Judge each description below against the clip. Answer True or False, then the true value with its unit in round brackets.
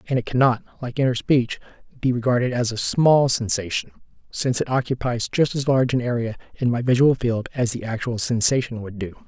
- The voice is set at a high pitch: False (120 Hz)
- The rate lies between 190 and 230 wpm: True (195 wpm)